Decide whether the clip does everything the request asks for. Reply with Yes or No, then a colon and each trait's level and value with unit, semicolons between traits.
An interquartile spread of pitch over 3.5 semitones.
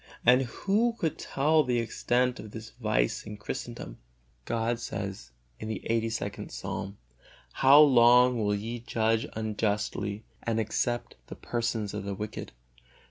No: average, 2.8 semitones